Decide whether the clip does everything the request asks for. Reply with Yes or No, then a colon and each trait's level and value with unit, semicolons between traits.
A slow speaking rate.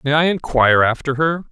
No: average, 200 wpm